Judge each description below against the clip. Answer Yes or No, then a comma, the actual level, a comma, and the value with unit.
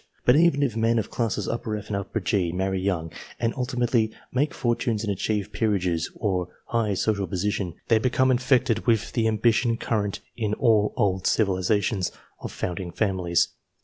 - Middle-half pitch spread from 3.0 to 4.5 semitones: Yes, average, 3.5 semitones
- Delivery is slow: No, average, 155 wpm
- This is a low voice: Yes, low, 105 Hz